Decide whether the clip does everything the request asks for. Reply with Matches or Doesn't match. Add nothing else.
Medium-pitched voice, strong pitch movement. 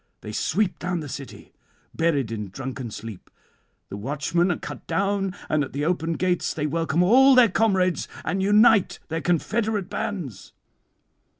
Matches